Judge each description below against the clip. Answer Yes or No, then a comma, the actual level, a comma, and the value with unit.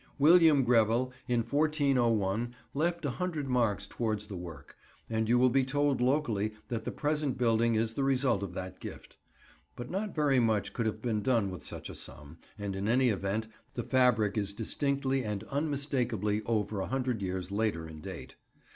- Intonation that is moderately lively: Yes, average, 4.5 semitones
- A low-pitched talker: Yes, low, 115 Hz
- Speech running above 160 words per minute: Yes, average, 180 wpm